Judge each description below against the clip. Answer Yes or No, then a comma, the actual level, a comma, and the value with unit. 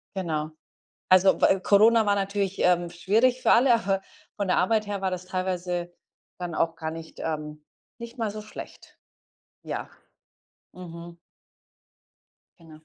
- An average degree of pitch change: Yes, average, 3.2 semitones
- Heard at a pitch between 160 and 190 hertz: Yes, medium, 185 Hz